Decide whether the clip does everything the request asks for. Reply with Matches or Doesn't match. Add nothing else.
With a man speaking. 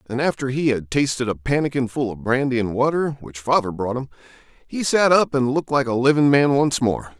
Matches